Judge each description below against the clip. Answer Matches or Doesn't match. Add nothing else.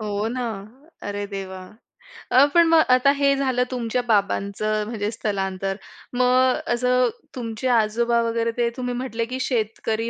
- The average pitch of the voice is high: Matches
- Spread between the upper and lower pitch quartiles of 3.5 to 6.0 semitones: Doesn't match